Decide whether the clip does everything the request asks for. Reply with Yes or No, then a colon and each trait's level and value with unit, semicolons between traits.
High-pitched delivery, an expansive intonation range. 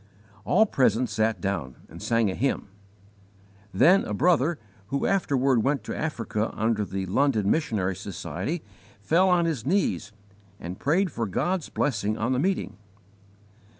No: low, 120 Hz; wide, 7.3 semitones